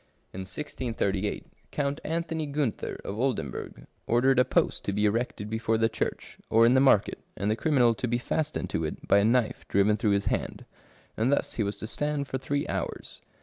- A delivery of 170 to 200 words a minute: Yes, average, 195 wpm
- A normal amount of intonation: Yes, average, 4.7 semitones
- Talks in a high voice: No, low, 115 Hz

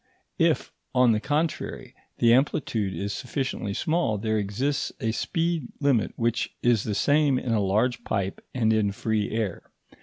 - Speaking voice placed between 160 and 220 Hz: No, low, 115 Hz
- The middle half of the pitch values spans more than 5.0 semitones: No, average, 4.4 semitones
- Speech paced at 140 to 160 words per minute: Yes, average, 155 wpm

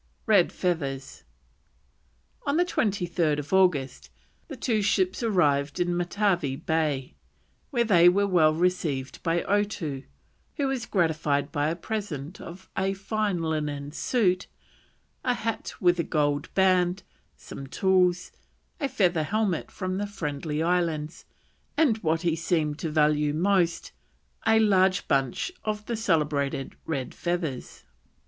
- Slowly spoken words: Yes, slow, 130 wpm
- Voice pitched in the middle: Yes, medium, 175 Hz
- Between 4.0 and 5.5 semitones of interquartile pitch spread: Yes, average, 4.8 semitones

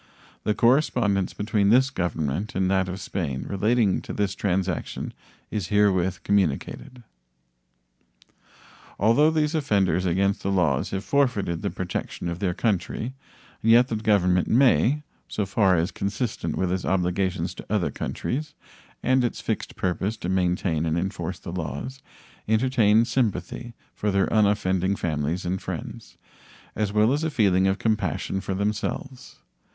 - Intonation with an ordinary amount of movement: Yes, average, 3.8 semitones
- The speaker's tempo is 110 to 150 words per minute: Yes, average, 140 wpm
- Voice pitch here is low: Yes, low, 100 Hz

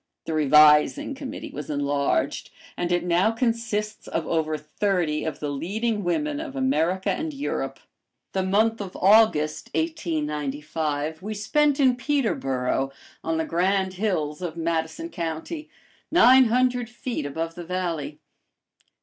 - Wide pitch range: Yes, wide, 7.2 semitones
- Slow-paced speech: Yes, slow, 130 wpm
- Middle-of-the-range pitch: Yes, medium, 180 Hz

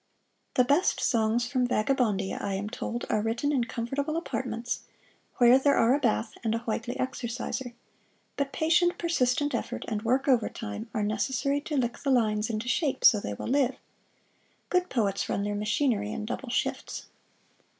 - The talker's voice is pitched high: Yes, high, 240 Hz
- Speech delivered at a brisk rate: No, average, 165 wpm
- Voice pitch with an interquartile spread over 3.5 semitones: Yes, average, 3.9 semitones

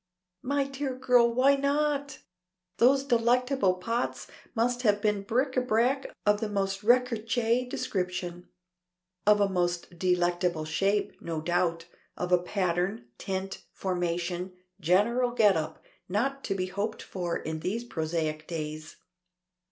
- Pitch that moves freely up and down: Yes, wide, 5.7 semitones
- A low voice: No, high, 200 Hz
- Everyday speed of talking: No, slow, 130 wpm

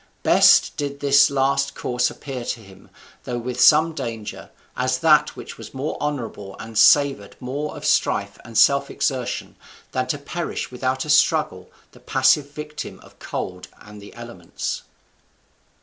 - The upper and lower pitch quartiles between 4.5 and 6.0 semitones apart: No, average, 3.3 semitones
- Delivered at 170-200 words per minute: No, average, 150 wpm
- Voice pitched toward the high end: No, low, 130 Hz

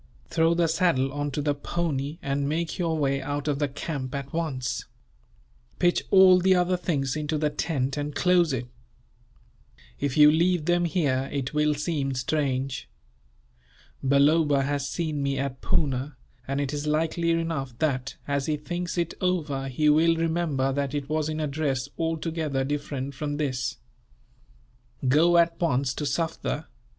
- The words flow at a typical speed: Yes, average, 160 wpm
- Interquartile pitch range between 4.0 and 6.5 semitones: No, average, 3.1 semitones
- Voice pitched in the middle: Yes, medium, 150 Hz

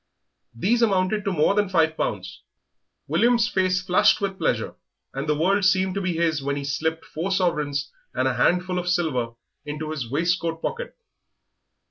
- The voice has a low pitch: No, medium, 175 Hz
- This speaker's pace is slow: No, average, 165 wpm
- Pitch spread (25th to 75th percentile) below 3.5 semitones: No, average, 4.0 semitones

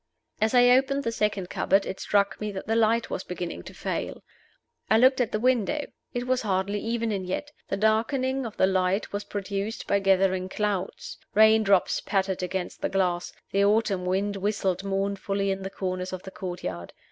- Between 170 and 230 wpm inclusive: Yes, average, 185 wpm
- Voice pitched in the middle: No, high, 200 Hz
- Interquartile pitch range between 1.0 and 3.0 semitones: Yes, average, 2.7 semitones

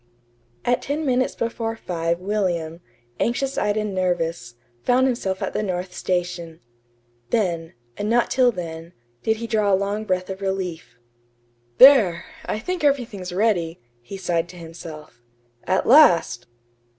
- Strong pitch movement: No, average, 4.9 semitones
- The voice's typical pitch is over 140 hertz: Yes, high, 190 Hz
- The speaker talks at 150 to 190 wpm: No, average, 140 wpm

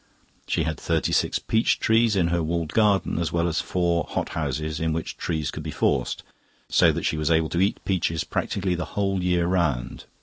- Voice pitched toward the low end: Yes, very low, 85 Hz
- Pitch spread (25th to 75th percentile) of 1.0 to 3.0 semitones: Yes, average, 2.7 semitones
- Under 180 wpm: No, fast, 205 wpm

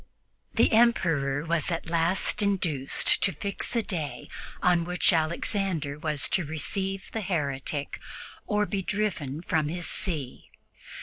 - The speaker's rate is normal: No, slow, 130 wpm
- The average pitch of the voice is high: No, medium, 170 Hz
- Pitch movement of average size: Yes, average, 4.6 semitones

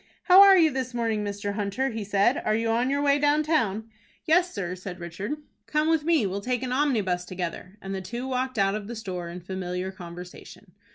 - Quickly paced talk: Yes, fast, 220 wpm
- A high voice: Yes, high, 220 Hz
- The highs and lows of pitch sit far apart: Yes, wide, 6.0 semitones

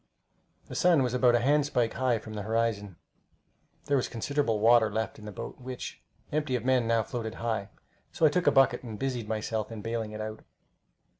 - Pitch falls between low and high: No, low, 115 Hz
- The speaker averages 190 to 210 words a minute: Yes, average, 200 wpm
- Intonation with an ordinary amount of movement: Yes, average, 3.0 semitones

